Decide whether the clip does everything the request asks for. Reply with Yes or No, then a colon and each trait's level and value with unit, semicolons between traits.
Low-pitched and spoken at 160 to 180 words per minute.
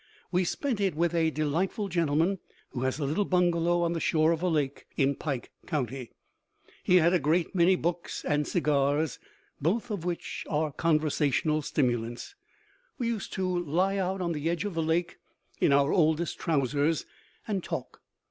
No: medium, 165 Hz; average, 170 wpm